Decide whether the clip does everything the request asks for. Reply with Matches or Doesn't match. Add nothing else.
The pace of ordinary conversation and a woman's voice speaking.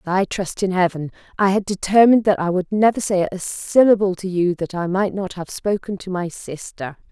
Doesn't match